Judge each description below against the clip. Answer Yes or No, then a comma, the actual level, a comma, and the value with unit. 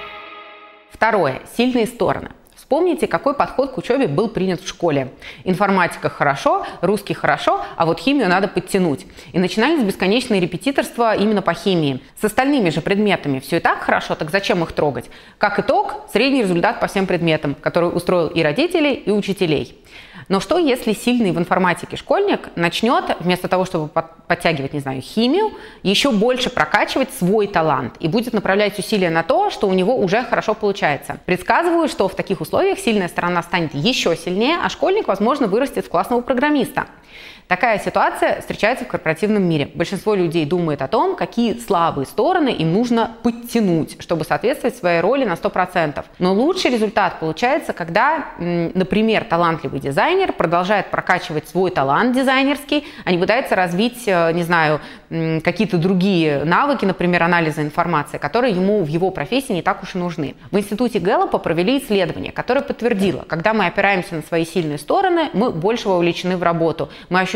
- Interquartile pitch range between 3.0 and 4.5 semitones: No, average, 5.2 semitones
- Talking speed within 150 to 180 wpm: Yes, fast, 160 wpm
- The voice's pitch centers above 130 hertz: Yes, high, 190 Hz